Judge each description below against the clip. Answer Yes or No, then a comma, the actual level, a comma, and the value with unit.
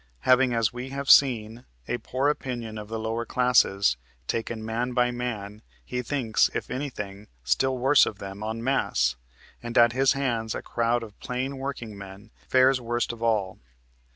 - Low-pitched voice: Yes, low, 120 Hz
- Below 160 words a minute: No, average, 170 wpm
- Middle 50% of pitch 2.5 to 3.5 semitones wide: Yes, average, 2.8 semitones